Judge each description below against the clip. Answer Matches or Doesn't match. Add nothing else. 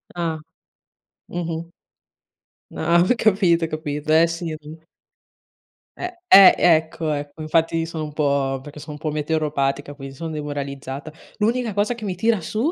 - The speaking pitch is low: Doesn't match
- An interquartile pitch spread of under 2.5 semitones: Doesn't match